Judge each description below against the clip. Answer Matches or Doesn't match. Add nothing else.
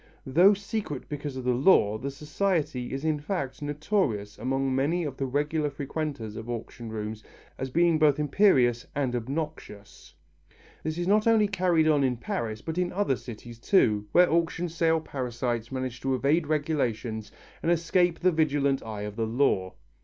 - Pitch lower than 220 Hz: Matches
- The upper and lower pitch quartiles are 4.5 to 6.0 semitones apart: Matches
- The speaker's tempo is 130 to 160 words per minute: Doesn't match